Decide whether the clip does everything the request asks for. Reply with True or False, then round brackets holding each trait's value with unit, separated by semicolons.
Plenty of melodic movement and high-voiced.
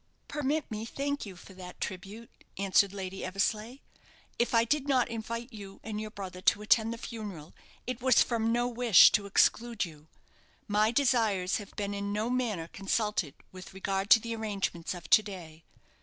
False (3.3 semitones; 210 Hz)